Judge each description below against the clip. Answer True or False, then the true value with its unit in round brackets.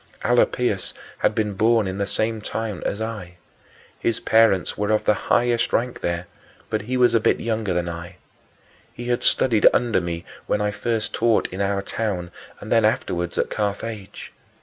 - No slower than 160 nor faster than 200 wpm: True (175 wpm)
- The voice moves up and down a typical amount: True (3.0 semitones)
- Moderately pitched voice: False (105 Hz)